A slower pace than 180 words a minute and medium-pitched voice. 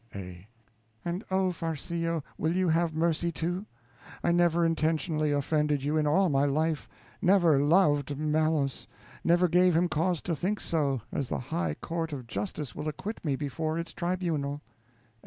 Yes: average, 155 wpm; medium, 160 Hz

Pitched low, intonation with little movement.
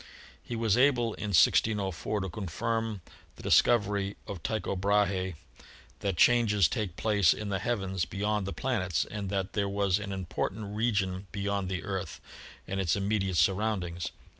Yes: low, 100 Hz; narrow, 2.1 semitones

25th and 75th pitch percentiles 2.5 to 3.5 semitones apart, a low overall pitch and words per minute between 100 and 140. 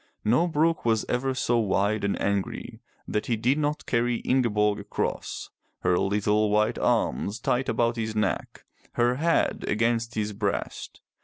No: average, 2.8 semitones; low, 115 Hz; average, 150 wpm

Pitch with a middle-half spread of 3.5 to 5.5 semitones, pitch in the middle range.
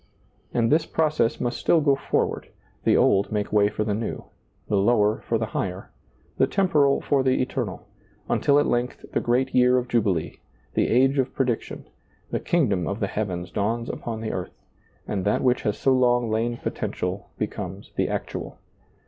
No: average, 4.0 semitones; low, 115 Hz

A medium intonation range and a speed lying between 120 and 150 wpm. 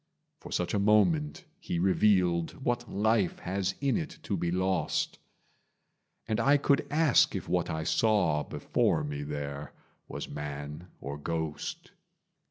No: wide, 7.1 semitones; average, 140 wpm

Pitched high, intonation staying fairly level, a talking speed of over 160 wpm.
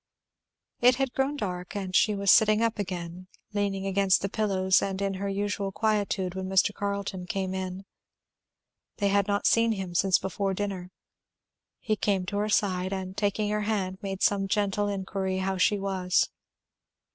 Yes: high, 195 Hz; narrow, 1.5 semitones; average, 170 wpm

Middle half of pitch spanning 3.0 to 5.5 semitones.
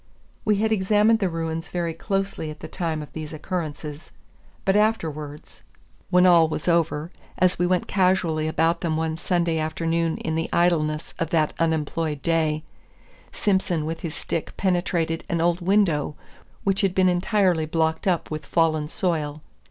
No: narrow, 2.5 semitones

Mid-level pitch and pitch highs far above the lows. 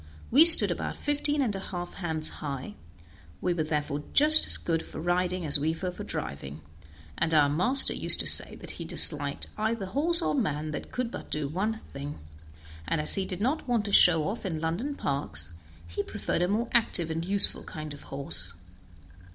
Yes: medium, 175 Hz; wide, 6.7 semitones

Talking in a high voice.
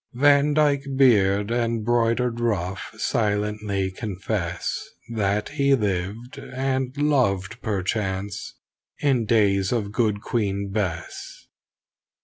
No: low, 105 Hz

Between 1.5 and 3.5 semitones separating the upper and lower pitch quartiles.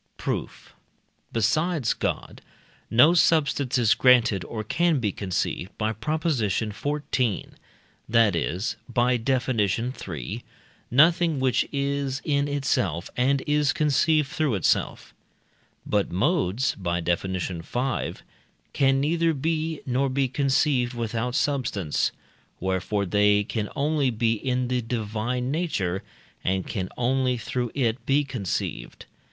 No: average, 5.2 semitones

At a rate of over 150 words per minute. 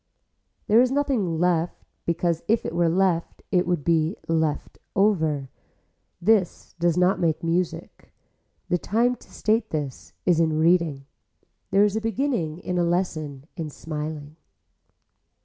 No: average, 140 wpm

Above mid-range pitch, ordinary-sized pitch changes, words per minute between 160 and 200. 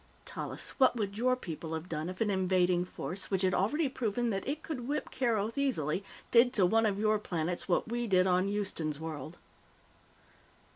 Yes: high, 200 Hz; average, 4.8 semitones; average, 185 wpm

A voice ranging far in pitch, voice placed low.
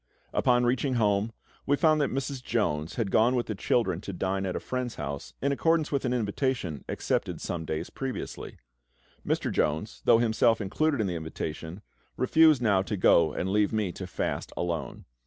Yes: wide, 5.9 semitones; low, 110 Hz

